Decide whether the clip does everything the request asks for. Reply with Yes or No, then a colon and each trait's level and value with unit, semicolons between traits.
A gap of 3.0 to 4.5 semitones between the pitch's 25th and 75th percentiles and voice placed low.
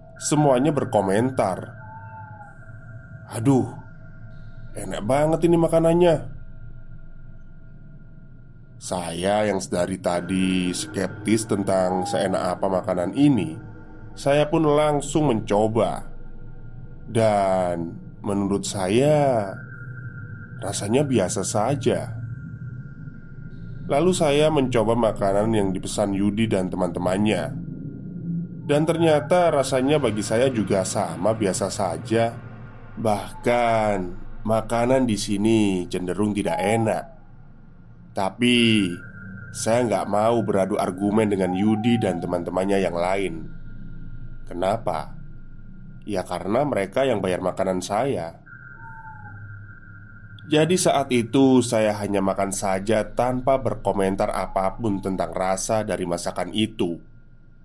No: average, 4.9 semitones; low, 115 Hz